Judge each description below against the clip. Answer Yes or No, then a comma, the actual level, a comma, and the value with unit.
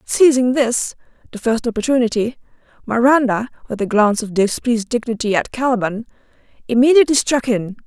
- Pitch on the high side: Yes, high, 235 Hz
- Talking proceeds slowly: Yes, slow, 130 wpm